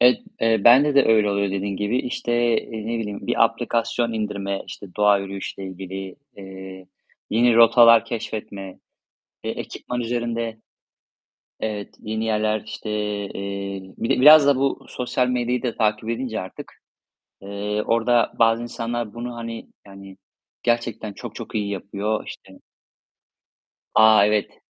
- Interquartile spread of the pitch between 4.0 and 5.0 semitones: No, average, 2.8 semitones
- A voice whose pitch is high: No, low, 110 Hz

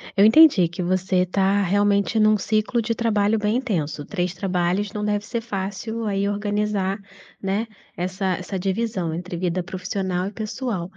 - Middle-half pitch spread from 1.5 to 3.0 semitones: Yes, narrow, 2.5 semitones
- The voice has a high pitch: Yes, high, 200 Hz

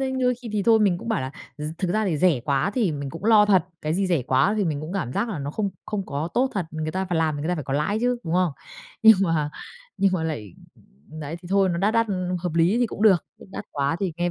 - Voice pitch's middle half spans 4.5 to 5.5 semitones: Yes, average, 5.1 semitones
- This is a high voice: No, medium, 180 Hz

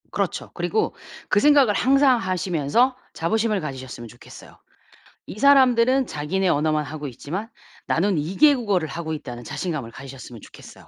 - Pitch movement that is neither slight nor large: No, wide, 8.3 semitones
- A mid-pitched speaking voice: Yes, medium, 180 Hz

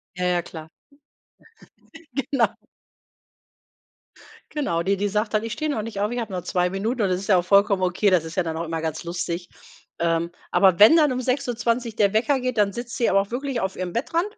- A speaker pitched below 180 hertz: No, high, 200 Hz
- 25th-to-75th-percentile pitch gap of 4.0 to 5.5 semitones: Yes, average, 5.0 semitones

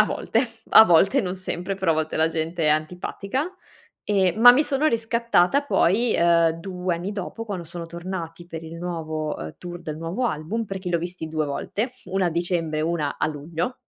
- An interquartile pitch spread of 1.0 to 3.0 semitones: No, average, 3.5 semitones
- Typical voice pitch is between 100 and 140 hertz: No, medium, 175 Hz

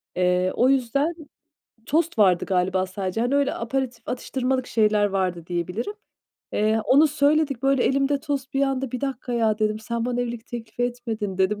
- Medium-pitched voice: No, high, 240 Hz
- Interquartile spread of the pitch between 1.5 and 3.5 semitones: No, average, 4.7 semitones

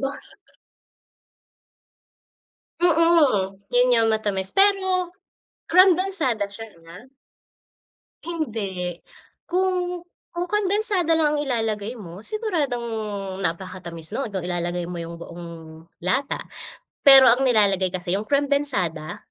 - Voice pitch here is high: Yes, high, 245 Hz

